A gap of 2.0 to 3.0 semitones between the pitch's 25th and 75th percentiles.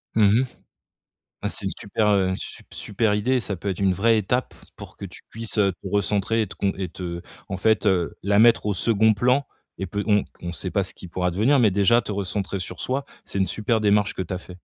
Yes: average, 2.7 semitones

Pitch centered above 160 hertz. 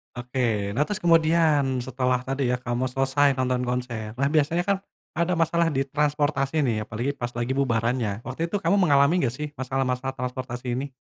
No: low, 135 Hz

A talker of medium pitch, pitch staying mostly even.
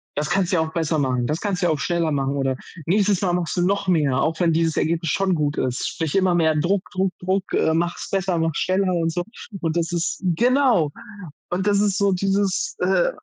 No: medium, 175 Hz; average, 3.3 semitones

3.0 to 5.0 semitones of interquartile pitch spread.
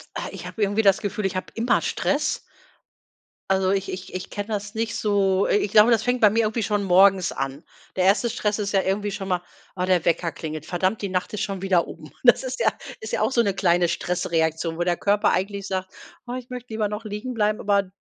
No: narrow, 2.5 semitones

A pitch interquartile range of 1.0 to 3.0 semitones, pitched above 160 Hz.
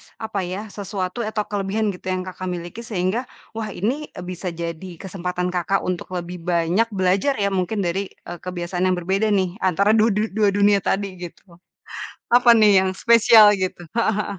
Yes: average, 2.7 semitones; high, 190 Hz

